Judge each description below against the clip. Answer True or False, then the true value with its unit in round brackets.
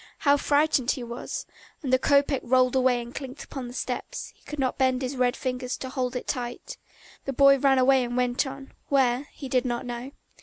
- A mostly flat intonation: True (1.7 semitones)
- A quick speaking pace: True (215 wpm)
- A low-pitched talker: False (260 Hz)